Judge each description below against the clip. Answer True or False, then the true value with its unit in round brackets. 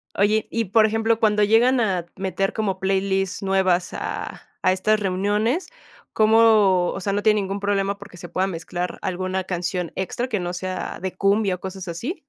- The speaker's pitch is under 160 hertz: False (195 Hz)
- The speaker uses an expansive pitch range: False (2.6 semitones)